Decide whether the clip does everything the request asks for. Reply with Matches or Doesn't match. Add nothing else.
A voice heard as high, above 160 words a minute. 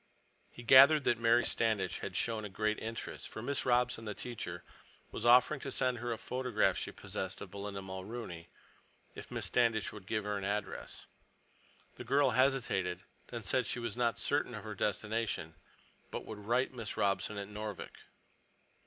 Doesn't match